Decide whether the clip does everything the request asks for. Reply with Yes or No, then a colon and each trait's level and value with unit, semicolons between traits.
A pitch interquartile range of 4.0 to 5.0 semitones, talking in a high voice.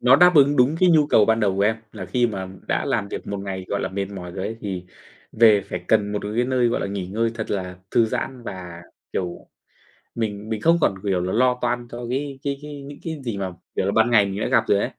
No: average, 4.3 semitones; low, 110 Hz